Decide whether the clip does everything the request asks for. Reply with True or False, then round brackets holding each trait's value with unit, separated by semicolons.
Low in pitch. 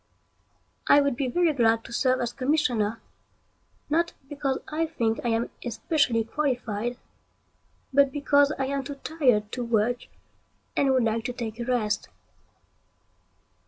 False (255 Hz)